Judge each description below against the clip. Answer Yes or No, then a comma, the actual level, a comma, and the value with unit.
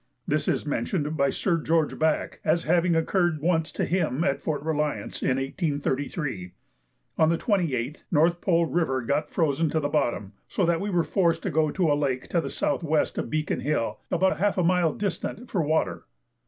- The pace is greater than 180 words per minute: Yes, average, 190 wpm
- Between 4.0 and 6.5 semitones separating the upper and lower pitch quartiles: No, average, 3.1 semitones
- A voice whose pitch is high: No, medium, 160 Hz